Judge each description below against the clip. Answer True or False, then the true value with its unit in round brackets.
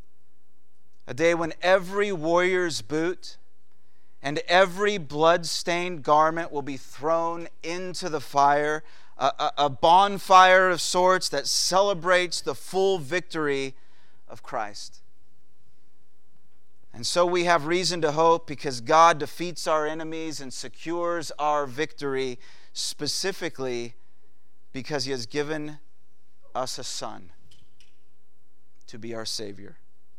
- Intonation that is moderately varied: False (7.0 semitones)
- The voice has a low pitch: False (150 Hz)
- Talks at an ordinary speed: False (110 wpm)